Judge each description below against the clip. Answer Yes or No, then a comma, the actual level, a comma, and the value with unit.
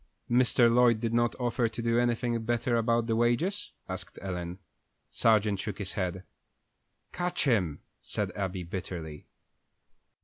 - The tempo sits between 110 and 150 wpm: Yes, slow, 135 wpm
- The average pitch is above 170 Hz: No, low, 115 Hz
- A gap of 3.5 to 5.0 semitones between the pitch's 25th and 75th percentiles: Yes, average, 3.9 semitones